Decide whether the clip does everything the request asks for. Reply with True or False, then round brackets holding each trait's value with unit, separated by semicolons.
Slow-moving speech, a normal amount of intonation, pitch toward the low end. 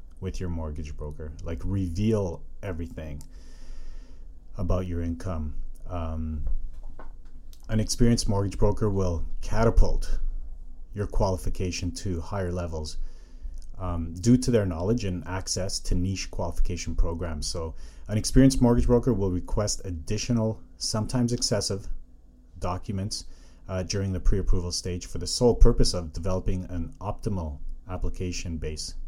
True (125 wpm; 4.4 semitones; 90 Hz)